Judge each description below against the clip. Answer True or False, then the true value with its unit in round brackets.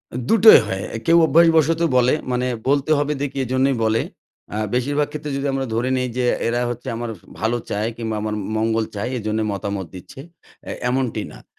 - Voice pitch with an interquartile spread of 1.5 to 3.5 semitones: False (4.3 semitones)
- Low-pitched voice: True (125 Hz)